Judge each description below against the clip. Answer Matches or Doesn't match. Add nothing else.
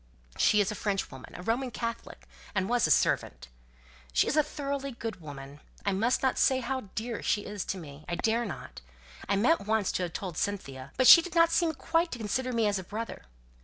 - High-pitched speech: Matches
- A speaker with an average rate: Doesn't match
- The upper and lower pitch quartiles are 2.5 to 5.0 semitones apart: Doesn't match